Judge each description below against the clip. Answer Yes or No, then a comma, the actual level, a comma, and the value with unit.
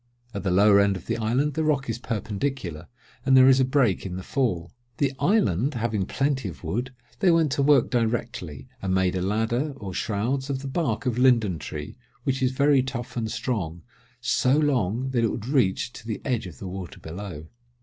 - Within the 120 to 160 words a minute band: No, fast, 205 wpm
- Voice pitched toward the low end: Yes, low, 120 Hz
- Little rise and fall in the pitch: No, wide, 5.5 semitones